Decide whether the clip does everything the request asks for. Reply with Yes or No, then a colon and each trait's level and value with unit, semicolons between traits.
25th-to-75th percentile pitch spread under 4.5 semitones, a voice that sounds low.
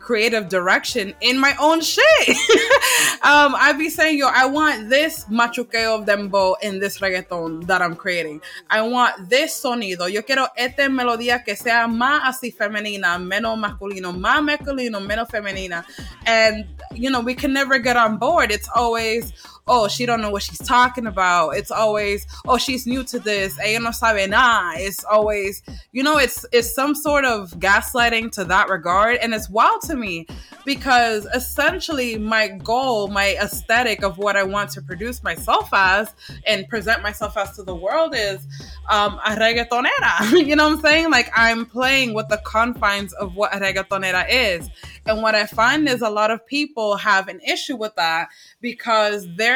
No: average, 4.1 semitones; high, 225 Hz